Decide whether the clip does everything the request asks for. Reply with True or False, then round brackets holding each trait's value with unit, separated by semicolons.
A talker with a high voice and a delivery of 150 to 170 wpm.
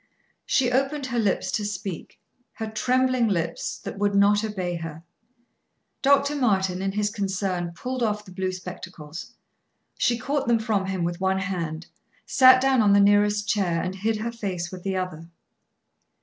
True (200 Hz; 165 wpm)